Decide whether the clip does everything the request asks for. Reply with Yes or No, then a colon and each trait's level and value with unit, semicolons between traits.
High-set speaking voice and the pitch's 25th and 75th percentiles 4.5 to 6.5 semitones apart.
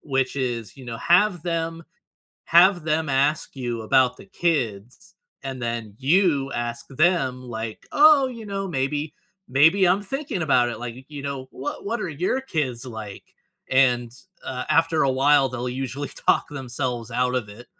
No: low, 135 Hz; average, 5.2 semitones